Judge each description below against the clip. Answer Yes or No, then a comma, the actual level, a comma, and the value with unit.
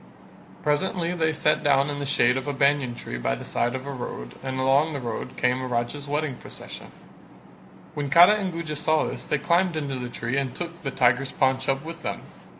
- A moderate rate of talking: No, fast, 215 wpm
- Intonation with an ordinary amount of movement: Yes, average, 3.4 semitones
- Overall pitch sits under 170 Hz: Yes, medium, 140 Hz